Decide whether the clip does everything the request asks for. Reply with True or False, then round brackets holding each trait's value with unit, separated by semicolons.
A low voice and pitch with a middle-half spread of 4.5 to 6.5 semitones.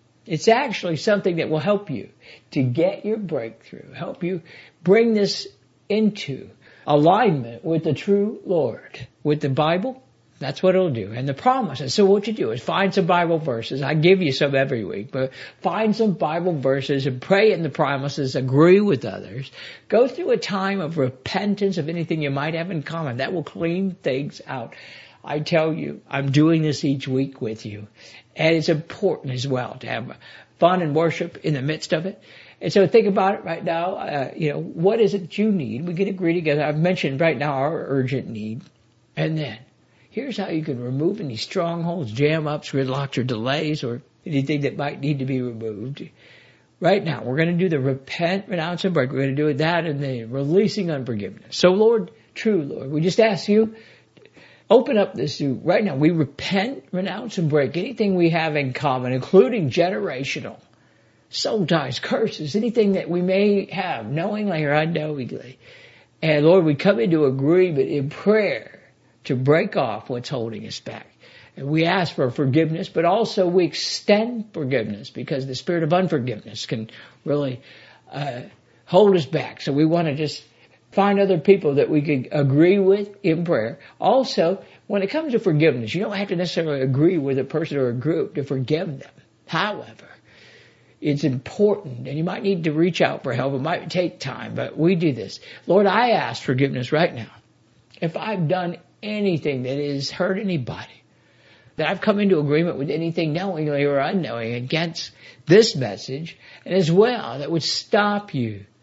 False (160 Hz; 5.6 semitones)